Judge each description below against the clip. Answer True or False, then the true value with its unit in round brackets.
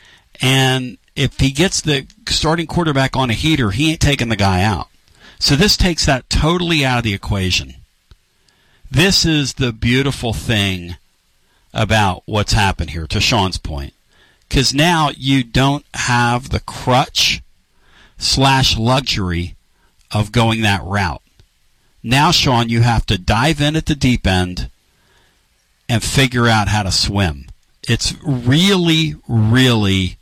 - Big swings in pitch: True (5.9 semitones)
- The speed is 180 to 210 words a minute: False (140 wpm)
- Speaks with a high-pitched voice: False (120 Hz)